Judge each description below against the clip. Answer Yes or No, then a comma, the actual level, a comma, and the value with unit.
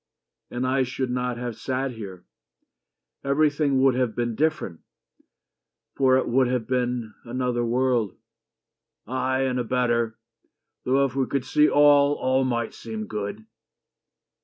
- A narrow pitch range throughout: Yes, narrow, 2.1 semitones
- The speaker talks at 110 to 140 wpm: Yes, slow, 135 wpm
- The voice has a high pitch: No, low, 125 Hz